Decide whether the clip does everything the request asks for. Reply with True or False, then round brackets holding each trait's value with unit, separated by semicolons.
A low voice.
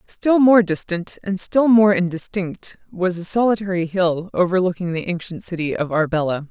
False (185 Hz)